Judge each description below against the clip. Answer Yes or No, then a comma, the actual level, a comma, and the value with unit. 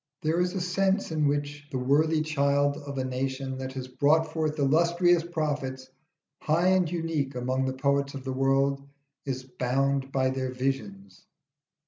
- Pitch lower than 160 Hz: Yes, medium, 140 Hz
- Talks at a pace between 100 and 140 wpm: No, average, 160 wpm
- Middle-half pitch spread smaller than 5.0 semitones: Yes, average, 3.2 semitones